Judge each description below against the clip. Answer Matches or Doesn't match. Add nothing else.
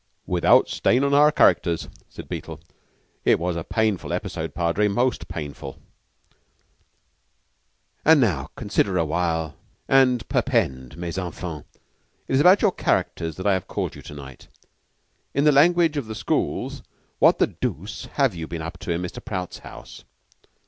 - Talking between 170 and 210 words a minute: Doesn't match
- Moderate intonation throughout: Doesn't match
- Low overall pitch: Matches